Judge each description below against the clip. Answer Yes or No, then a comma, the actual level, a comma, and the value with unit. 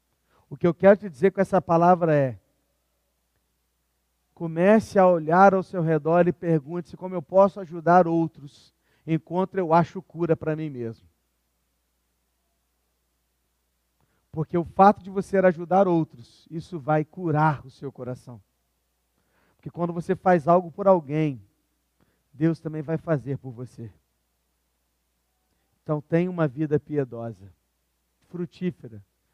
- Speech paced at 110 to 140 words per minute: Yes, average, 125 wpm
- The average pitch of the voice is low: No, medium, 150 Hz